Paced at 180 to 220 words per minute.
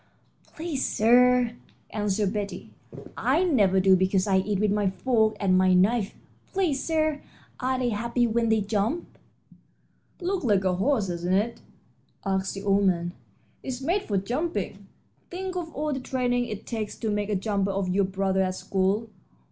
No: average, 165 wpm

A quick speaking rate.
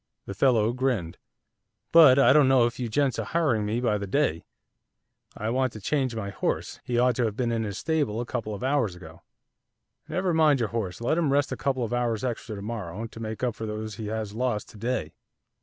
Yes: fast, 225 wpm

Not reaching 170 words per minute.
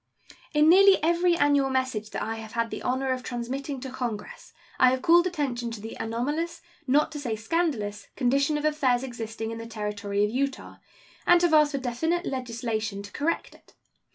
No: average, 185 wpm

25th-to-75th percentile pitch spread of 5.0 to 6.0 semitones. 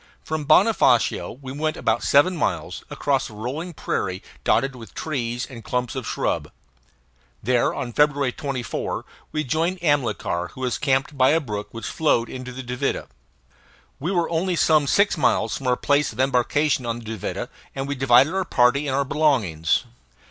No: average, 4.0 semitones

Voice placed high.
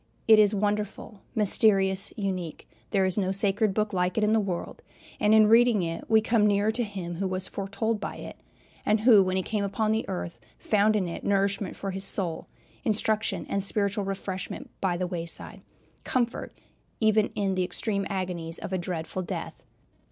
Yes: high, 200 Hz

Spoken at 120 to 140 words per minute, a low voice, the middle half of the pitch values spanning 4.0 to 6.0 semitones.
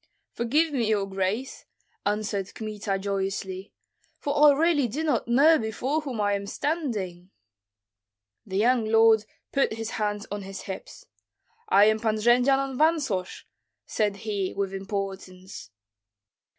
No: slow, 135 wpm; high, 215 Hz; average, 5.1 semitones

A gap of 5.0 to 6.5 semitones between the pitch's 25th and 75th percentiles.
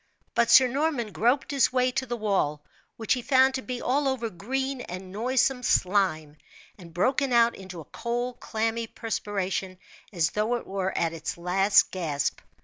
Yes: average, 5.3 semitones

